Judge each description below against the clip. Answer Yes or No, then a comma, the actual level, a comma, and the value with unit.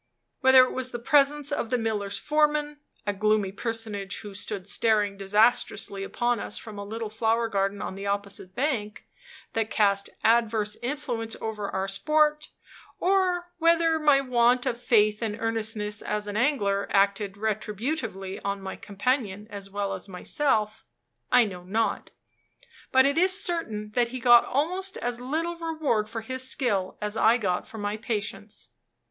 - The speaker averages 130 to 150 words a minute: No, average, 160 wpm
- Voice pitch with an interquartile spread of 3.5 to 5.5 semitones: Yes, average, 4.2 semitones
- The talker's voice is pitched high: Yes, high, 225 Hz